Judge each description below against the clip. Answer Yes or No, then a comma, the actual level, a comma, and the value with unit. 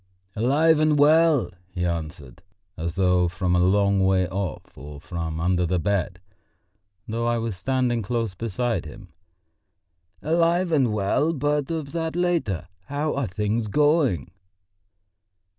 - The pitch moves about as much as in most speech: No, wide, 8.5 semitones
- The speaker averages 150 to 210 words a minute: No, slow, 135 wpm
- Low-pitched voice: Yes, low, 110 Hz